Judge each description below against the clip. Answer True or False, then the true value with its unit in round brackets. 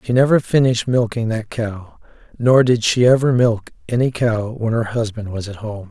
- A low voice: True (115 Hz)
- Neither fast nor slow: True (195 wpm)